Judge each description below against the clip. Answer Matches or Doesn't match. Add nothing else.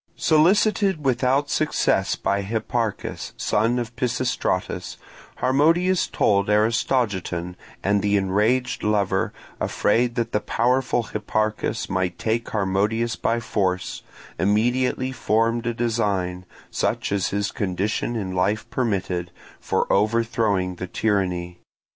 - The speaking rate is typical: Doesn't match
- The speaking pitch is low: Matches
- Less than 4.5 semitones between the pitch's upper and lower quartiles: Matches